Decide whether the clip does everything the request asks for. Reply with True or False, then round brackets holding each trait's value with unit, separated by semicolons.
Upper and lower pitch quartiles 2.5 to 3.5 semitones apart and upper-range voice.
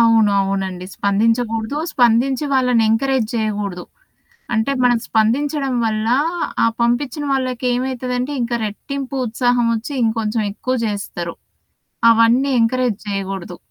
True (2.9 semitones; 230 Hz)